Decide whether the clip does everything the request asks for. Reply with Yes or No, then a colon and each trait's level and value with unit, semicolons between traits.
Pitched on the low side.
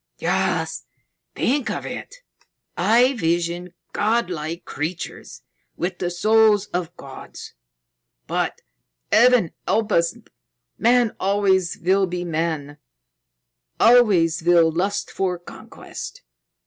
No: medium, 180 Hz